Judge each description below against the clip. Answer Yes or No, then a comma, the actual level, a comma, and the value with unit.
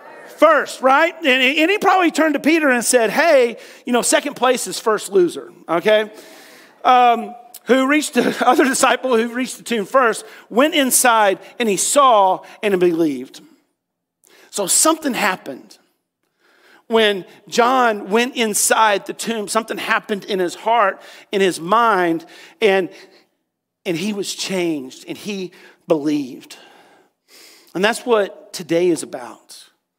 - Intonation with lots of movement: Yes, wide, 5.9 semitones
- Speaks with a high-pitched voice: Yes, high, 235 Hz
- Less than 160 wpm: Yes, average, 140 wpm